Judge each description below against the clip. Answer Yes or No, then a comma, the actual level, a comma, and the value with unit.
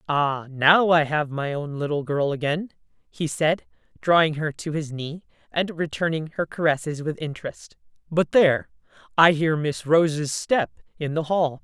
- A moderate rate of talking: Yes, average, 165 wpm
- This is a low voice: No, medium, 155 Hz